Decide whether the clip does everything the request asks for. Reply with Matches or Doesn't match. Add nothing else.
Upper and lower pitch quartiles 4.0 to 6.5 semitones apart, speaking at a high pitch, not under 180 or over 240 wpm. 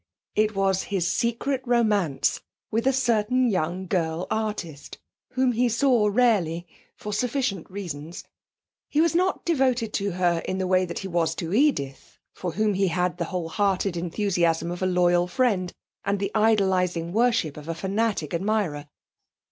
Doesn't match